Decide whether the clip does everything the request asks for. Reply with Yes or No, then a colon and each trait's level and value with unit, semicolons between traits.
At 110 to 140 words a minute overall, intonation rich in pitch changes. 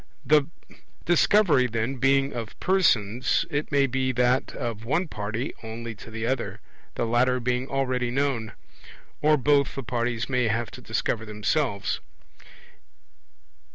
No: slow, 135 wpm; average, 3.1 semitones